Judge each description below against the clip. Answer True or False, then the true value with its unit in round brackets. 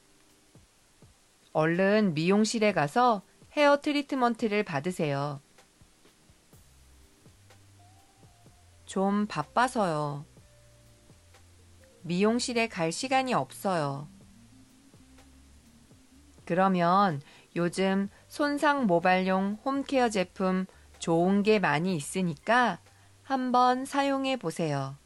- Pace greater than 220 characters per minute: False (165 characters per minute)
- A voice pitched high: False (175 Hz)